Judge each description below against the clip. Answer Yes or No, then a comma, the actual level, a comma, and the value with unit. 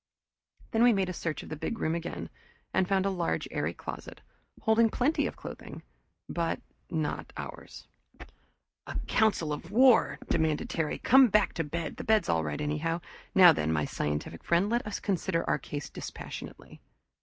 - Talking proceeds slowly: No, average, 175 wpm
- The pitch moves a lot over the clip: Yes, wide, 5.7 semitones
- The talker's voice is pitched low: No, medium, 170 Hz